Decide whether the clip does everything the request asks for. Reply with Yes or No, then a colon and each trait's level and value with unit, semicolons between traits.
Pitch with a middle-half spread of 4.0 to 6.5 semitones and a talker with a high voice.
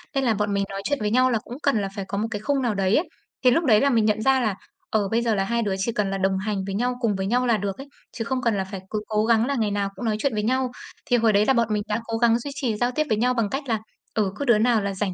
No: average, 3.3 semitones; high, 220 Hz